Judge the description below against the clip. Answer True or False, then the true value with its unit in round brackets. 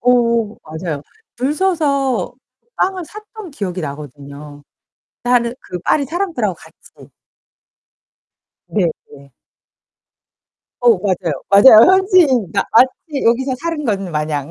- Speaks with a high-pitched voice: True (235 Hz)